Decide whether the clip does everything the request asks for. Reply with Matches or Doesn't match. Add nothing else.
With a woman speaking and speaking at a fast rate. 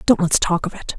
Matches